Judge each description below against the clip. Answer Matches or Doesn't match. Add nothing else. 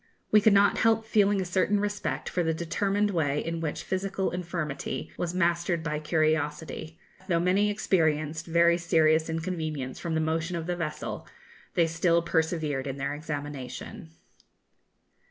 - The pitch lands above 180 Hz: Doesn't match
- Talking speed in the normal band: Matches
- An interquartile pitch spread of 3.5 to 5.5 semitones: Doesn't match